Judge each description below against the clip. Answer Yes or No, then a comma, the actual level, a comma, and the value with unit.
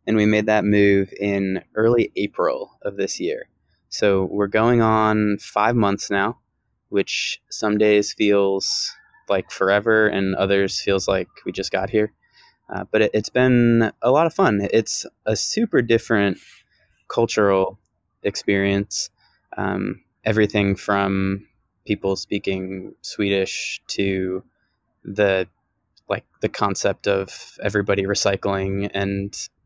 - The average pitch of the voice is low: Yes, low, 100 Hz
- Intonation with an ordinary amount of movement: No, narrow, 1.9 semitones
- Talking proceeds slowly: Yes, slow, 125 wpm